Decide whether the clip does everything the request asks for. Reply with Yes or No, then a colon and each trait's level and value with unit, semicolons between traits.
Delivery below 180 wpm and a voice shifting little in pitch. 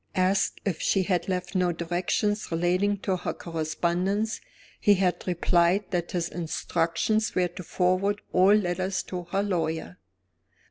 Yes: average, 140 wpm; narrow, 2.2 semitones